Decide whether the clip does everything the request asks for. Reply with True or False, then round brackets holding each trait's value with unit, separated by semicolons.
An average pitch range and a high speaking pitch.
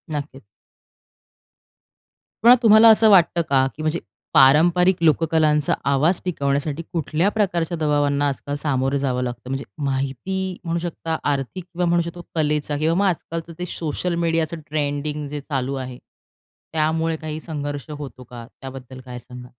False (3.4 semitones; 150 Hz)